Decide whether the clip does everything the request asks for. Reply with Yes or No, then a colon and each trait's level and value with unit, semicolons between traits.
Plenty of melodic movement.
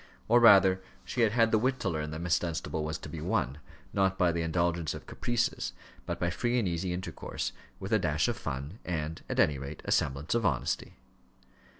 Yes: wide, 5.7 semitones